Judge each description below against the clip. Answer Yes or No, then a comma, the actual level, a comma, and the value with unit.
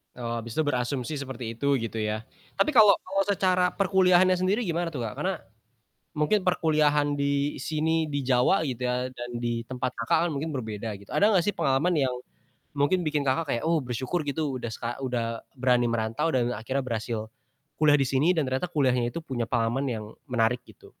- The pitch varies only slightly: No, average, 5.1 semitones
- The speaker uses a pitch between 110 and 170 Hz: Yes, low, 135 Hz